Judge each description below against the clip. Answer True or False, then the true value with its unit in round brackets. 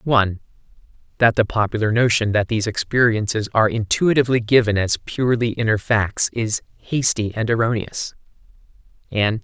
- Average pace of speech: False (125 wpm)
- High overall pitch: False (110 Hz)